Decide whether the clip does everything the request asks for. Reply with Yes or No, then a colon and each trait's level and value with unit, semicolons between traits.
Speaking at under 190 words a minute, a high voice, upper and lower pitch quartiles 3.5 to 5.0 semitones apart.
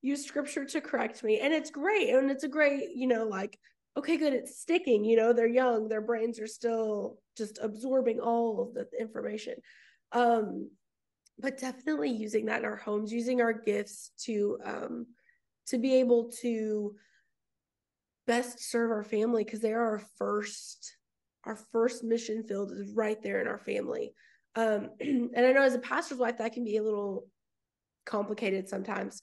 No: average, 170 wpm; high, 235 Hz; average, 3.0 semitones